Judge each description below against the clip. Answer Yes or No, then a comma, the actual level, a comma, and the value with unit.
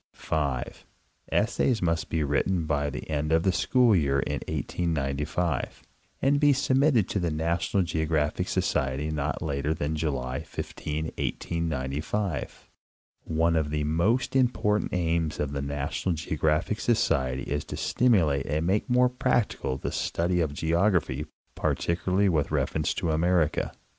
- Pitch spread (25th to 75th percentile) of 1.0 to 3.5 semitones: No, average, 4.0 semitones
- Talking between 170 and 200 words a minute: No, average, 140 wpm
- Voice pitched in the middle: No, very low, 80 Hz